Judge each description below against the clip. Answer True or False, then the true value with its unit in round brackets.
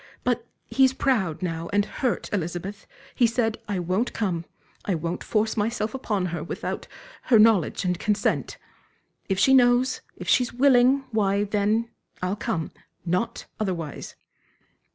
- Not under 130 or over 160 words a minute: True (140 wpm)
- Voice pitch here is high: True (210 Hz)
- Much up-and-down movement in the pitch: False (4.8 semitones)